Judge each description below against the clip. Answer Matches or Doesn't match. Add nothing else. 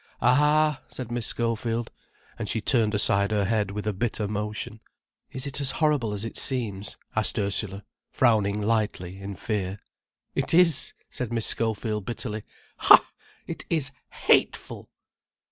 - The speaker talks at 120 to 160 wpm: Matches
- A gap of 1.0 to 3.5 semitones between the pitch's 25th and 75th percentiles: Matches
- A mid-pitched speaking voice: Doesn't match